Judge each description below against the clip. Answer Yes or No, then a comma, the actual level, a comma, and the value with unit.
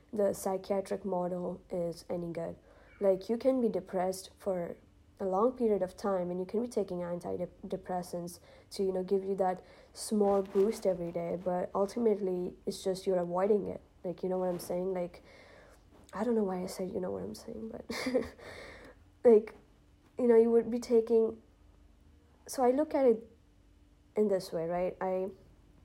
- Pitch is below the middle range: No, high, 190 Hz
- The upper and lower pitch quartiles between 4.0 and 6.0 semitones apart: No, average, 3.3 semitones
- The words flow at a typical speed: Yes, average, 175 wpm